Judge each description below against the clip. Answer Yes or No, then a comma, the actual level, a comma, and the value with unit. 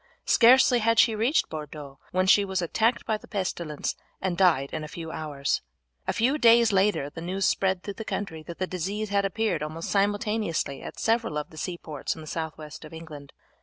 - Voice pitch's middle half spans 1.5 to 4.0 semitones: No, average, 5.2 semitones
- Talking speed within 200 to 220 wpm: Yes, fast, 205 wpm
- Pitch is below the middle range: No, medium, 185 Hz